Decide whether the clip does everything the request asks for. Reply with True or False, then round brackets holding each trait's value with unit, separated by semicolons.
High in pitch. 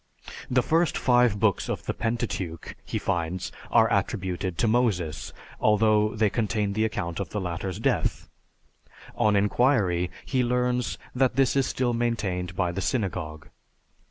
False (105 Hz)